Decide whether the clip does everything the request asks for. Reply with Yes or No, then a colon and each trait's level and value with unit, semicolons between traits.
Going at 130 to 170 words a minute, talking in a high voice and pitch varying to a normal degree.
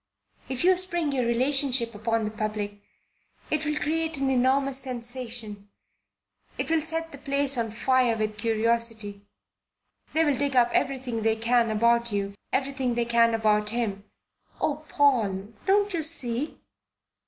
Yes: average, 140 wpm; high, 245 Hz; average, 4.0 semitones